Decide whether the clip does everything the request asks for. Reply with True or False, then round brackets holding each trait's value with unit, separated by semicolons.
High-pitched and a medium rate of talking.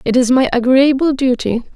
True (255 Hz; 170 wpm)